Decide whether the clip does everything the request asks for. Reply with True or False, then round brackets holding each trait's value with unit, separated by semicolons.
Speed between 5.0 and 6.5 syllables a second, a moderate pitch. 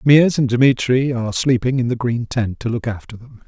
False (5.5 syllables/s; 120 Hz)